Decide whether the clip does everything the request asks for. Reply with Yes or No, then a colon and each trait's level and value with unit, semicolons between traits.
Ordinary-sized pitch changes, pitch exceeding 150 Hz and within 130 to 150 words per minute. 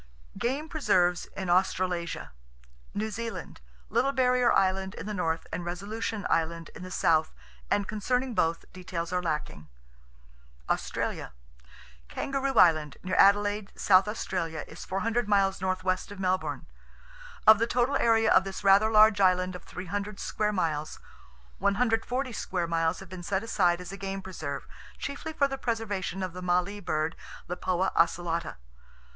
Yes: average, 3.6 semitones; high, 190 Hz; average, 145 wpm